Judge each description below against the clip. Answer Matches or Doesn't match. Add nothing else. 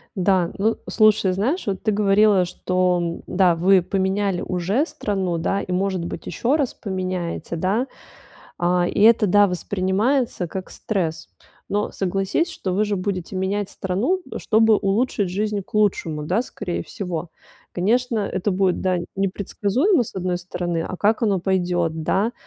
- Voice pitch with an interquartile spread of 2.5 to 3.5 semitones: Matches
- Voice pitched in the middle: Doesn't match